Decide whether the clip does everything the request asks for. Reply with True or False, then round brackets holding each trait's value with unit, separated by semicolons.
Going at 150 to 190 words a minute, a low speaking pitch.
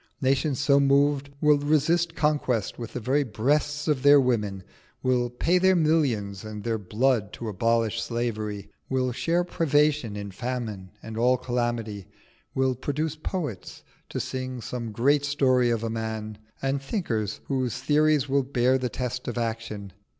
True (155 wpm; 125 Hz)